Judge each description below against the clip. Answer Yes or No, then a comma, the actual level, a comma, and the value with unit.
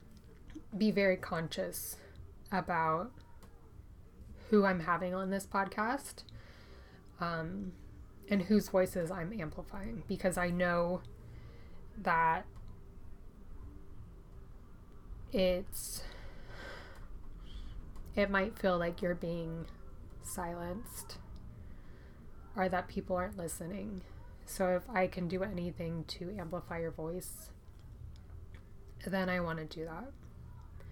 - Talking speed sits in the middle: No, slow, 95 wpm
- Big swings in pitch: Yes, wide, 9.0 semitones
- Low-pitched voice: No, medium, 175 Hz